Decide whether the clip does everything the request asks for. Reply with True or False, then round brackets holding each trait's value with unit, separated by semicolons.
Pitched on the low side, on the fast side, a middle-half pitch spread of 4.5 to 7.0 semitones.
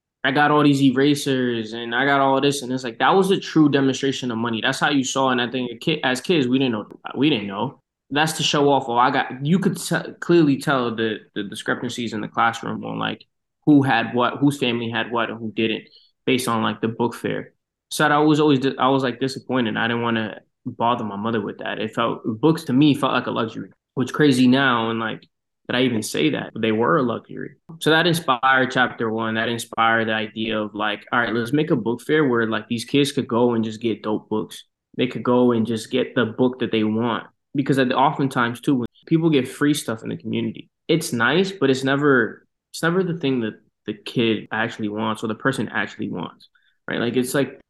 False (125 Hz; 240 wpm; 3.6 semitones)